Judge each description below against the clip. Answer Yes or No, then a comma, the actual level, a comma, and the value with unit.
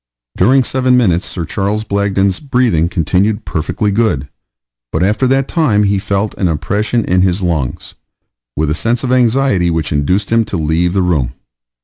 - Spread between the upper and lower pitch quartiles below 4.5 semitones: No, average, 5.2 semitones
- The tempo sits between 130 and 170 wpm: Yes, average, 165 wpm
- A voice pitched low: Yes, low, 100 Hz